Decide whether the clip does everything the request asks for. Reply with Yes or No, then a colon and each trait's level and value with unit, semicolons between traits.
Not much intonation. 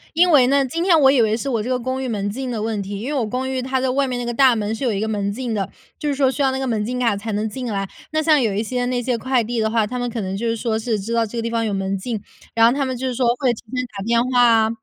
No: average, 3.0 semitones